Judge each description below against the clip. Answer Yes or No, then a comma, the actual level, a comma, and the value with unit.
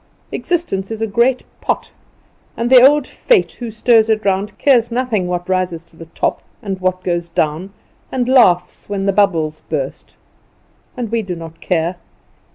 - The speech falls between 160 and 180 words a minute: Yes, average, 165 wpm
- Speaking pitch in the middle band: No, high, 195 Hz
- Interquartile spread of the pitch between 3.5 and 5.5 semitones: Yes, average, 5.2 semitones